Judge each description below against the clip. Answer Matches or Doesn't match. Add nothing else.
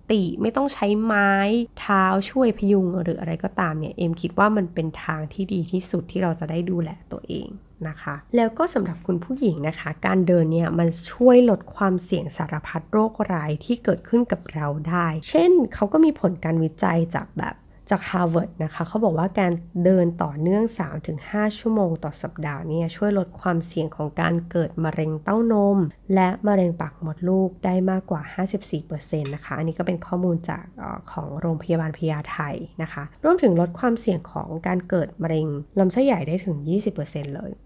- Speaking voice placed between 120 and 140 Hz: Doesn't match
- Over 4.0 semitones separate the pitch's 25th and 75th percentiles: Doesn't match